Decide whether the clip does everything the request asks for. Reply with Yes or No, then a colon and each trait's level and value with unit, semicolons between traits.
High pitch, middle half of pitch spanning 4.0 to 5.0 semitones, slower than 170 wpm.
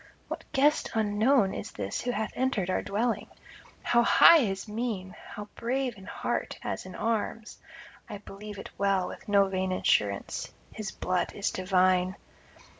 No: high, 205 Hz; average, 3.6 semitones; average, 155 wpm